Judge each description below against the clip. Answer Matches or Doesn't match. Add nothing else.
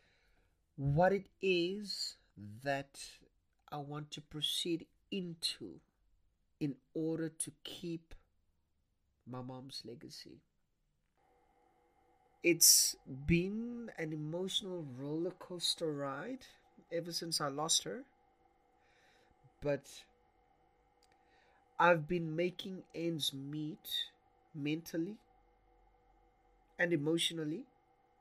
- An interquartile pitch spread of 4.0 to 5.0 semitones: Matches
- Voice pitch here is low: Doesn't match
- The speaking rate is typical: Doesn't match